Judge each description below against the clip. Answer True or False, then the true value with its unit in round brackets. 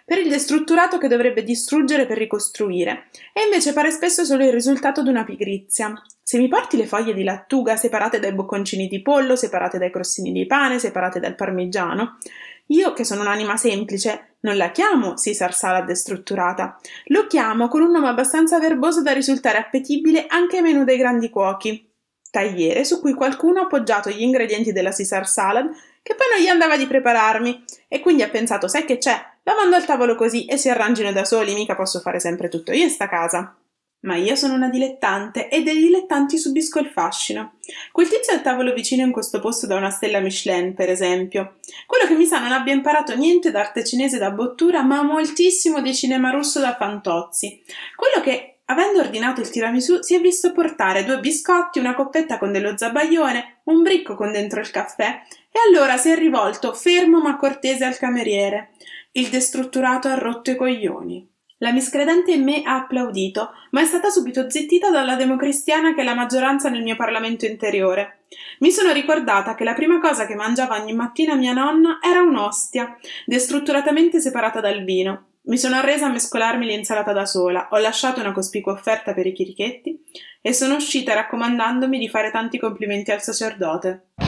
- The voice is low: False (250 Hz)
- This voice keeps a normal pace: False (185 wpm)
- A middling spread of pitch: False (6.2 semitones)